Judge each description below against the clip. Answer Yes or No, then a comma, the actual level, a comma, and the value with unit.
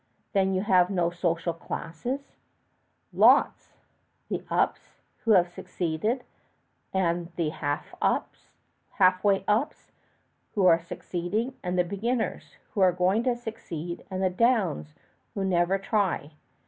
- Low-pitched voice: No, medium, 185 Hz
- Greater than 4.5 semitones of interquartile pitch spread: No, average, 3.3 semitones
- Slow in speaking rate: Yes, slow, 120 wpm